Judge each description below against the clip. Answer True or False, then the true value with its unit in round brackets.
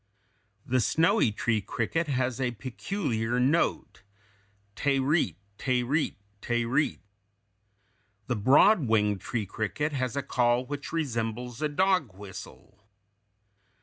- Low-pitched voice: True (125 Hz)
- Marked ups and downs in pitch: False (4.4 semitones)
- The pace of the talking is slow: True (115 wpm)